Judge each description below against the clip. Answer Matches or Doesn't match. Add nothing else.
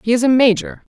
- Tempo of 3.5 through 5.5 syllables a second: Doesn't match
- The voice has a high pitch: Matches